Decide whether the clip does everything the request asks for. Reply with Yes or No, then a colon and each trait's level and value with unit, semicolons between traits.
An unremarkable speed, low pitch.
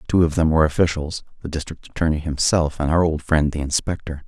Yes: average, 195 wpm; very low, 80 Hz